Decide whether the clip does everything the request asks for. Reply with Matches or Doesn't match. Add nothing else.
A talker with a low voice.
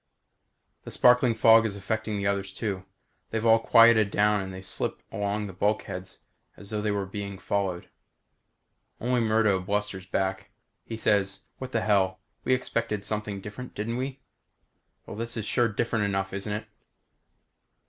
Matches